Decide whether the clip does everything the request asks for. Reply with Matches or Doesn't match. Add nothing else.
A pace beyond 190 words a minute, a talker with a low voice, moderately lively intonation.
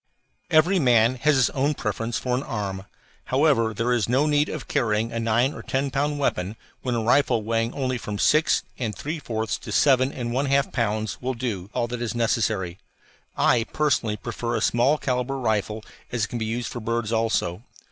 Matches